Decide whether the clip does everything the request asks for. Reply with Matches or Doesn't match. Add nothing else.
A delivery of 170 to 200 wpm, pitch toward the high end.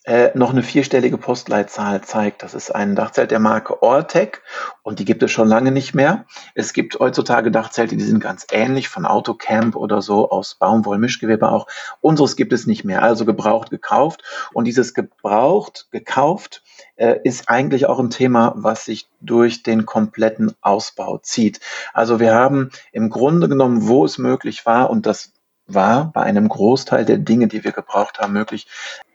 Doesn't match